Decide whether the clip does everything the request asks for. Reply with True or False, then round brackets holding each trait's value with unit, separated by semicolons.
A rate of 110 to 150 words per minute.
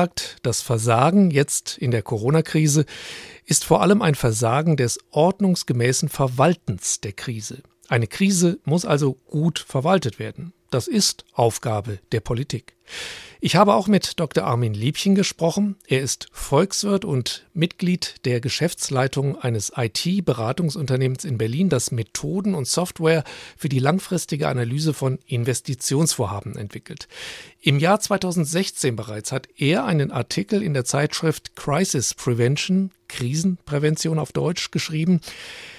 True (125 wpm)